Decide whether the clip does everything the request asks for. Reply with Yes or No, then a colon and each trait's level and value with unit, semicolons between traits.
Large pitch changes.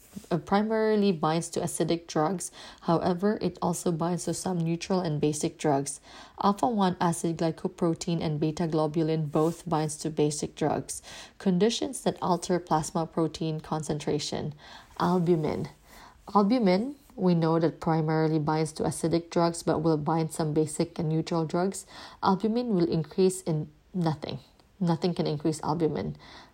No: narrow, 2.5 semitones